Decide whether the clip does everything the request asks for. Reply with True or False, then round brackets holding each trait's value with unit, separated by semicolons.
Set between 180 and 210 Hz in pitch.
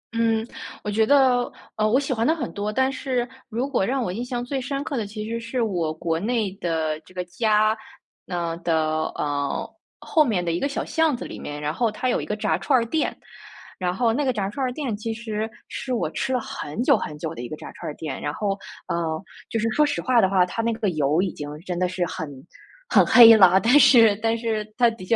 False (220 Hz)